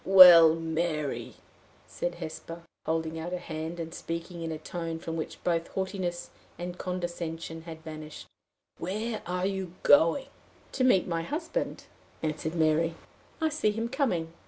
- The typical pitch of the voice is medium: Yes, medium, 170 Hz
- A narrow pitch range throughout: Yes, narrow, 2.2 semitones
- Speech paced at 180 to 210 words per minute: No, average, 145 wpm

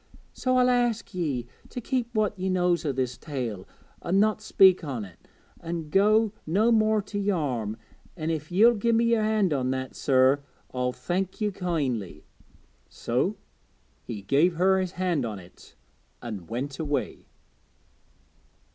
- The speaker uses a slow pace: No, average, 150 wpm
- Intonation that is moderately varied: No, wide, 8.2 semitones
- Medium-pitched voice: Yes, medium, 175 Hz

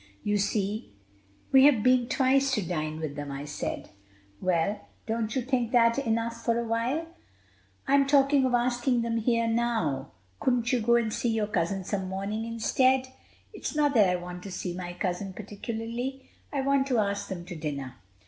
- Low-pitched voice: No, high, 230 Hz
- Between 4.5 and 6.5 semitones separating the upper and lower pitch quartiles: Yes, average, 4.9 semitones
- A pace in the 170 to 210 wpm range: Yes, average, 180 wpm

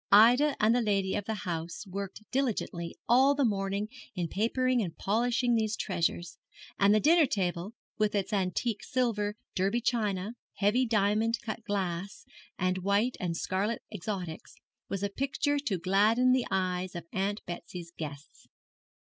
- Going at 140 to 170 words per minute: Yes, average, 150 wpm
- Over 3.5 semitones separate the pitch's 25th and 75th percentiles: Yes, average, 4.0 semitones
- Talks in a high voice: Yes, high, 205 Hz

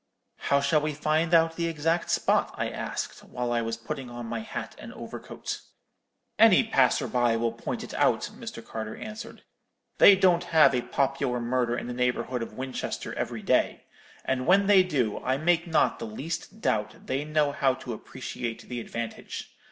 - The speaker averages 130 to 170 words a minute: No, average, 180 wpm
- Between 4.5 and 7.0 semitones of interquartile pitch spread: Yes, average, 5.2 semitones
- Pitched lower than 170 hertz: Yes, low, 135 Hz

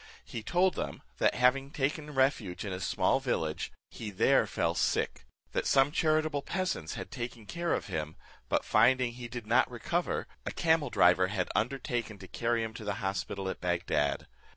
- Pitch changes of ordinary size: No, wide, 6.3 semitones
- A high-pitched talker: No, low, 120 Hz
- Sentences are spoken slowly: No, average, 175 wpm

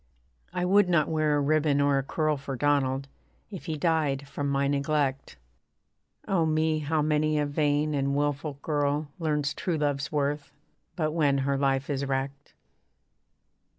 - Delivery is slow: No, average, 155 wpm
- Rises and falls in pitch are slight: Yes, narrow, 1.8 semitones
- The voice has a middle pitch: Yes, medium, 145 Hz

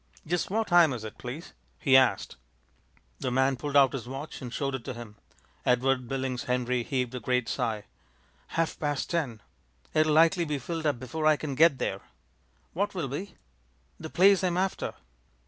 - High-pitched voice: No, low, 135 Hz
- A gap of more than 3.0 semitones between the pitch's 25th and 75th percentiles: Yes, average, 4.4 semitones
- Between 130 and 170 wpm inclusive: No, average, 180 wpm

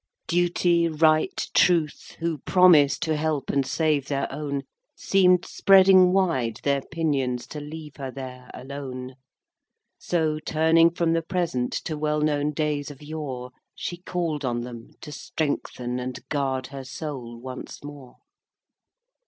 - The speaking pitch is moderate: Yes, medium, 150 Hz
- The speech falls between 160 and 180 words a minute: No, average, 140 wpm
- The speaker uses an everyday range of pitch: Yes, average, 3.7 semitones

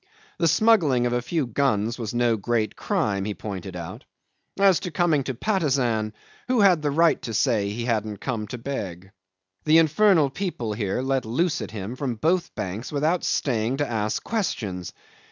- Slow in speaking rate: No, average, 175 wpm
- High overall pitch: No, low, 125 Hz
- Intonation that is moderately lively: No, wide, 6.5 semitones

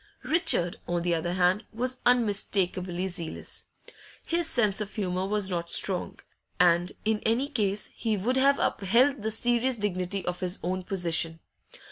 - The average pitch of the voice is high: Yes, high, 195 Hz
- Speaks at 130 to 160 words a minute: Yes, average, 150 wpm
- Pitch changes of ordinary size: Yes, average, 4.5 semitones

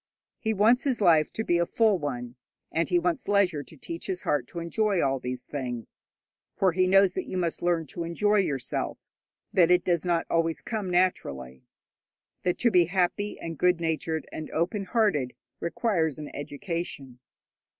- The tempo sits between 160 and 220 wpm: Yes, average, 175 wpm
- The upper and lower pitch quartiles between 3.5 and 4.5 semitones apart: Yes, average, 3.8 semitones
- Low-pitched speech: No, medium, 170 Hz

